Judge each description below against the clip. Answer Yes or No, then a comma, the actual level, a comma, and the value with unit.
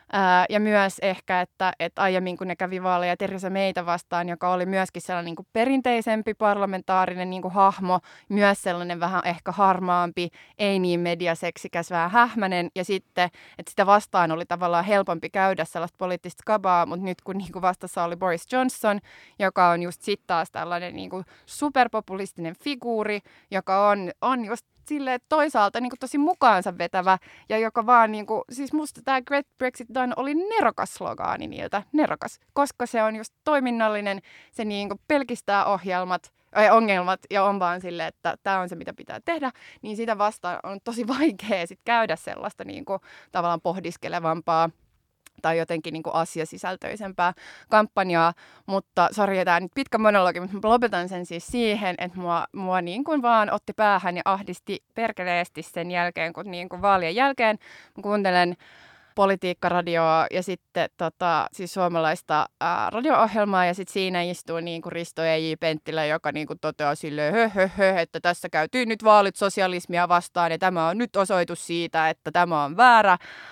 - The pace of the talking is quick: Yes, fast, 165 wpm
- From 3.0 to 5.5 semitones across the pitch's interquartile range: Yes, average, 3.6 semitones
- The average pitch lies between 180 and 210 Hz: Yes, medium, 185 Hz